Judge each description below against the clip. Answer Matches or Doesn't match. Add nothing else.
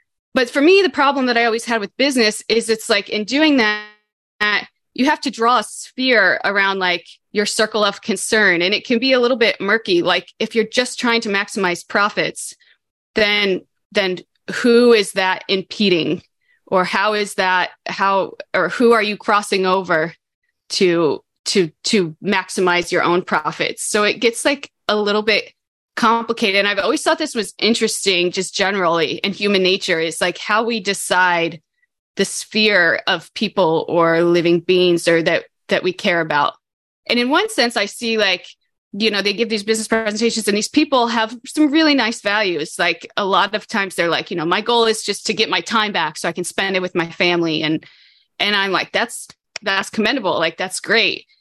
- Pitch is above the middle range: Matches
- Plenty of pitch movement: Doesn't match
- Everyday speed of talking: Matches